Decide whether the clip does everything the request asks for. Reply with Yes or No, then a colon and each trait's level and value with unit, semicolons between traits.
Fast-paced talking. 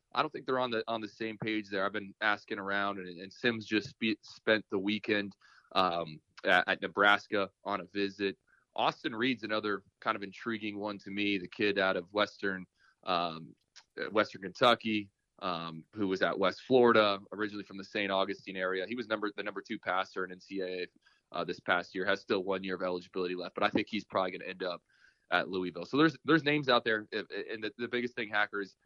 Yes: fast, 210 wpm